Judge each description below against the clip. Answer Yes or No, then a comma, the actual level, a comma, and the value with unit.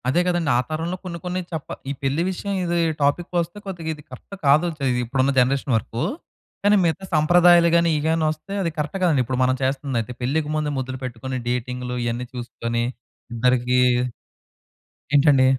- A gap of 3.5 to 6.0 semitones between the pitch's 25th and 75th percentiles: Yes, average, 5.1 semitones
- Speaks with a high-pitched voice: No, medium, 145 Hz